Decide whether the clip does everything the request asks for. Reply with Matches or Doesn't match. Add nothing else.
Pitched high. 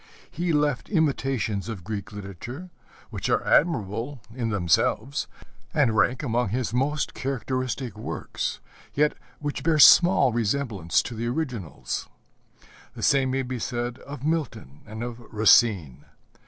Doesn't match